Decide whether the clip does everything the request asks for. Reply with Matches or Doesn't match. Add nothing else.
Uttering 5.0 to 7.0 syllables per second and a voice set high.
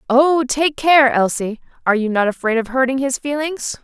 Matches